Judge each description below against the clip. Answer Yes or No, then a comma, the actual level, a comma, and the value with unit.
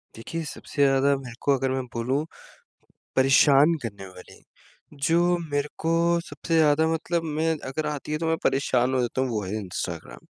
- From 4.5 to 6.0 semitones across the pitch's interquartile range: No, average, 4.1 semitones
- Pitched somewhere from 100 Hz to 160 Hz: Yes, medium, 140 Hz